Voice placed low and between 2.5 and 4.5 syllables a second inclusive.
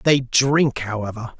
Yes: low, 125 Hz; 4.0 syllables/s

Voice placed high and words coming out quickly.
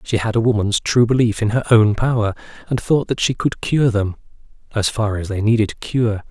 No: low, 110 Hz; fast, 210 wpm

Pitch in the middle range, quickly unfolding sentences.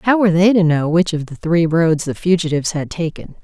Yes: medium, 170 Hz; fast, 245 wpm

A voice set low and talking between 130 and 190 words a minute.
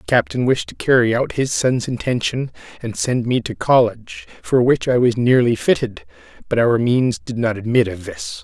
No: low, 120 Hz; average, 200 wpm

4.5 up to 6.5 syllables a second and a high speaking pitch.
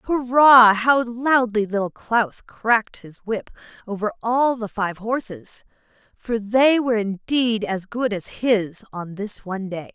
No: 3.9 syllables/s; high, 220 Hz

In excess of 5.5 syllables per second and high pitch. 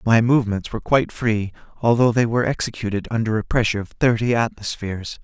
No: 6.4 syllables/s; low, 110 Hz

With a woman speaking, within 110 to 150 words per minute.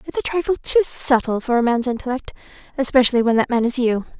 No: female; average, 200 wpm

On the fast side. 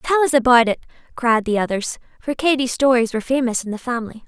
Yes: fast, 210 wpm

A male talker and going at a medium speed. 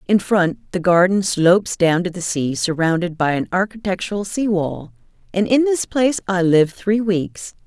No: female; average, 180 wpm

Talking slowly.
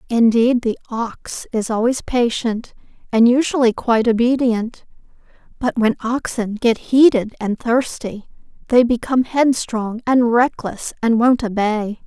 Yes: slow, 125 wpm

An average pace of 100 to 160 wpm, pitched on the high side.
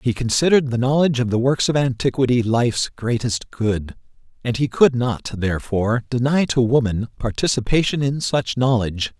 No: average, 155 wpm; low, 125 Hz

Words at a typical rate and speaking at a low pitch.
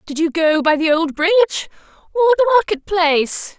No: average, 185 wpm; very high, 350 Hz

